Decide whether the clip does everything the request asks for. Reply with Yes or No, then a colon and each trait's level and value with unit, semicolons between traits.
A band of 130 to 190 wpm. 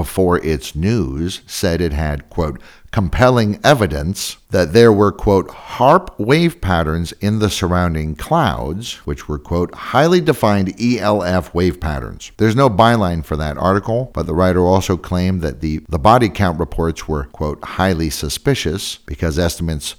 Yes: average, 155 wpm